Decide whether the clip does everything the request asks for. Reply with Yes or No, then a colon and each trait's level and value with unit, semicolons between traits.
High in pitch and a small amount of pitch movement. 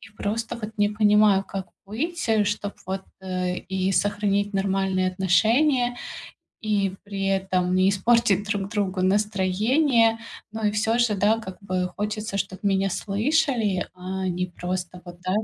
Yes: high, 200 Hz; narrow, 2.3 semitones